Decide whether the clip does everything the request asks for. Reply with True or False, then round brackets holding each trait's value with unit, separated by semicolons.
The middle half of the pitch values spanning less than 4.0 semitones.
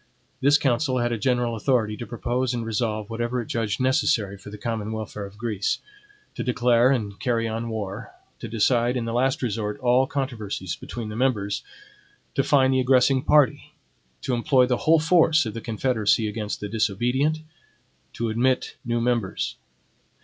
True (2.9 semitones)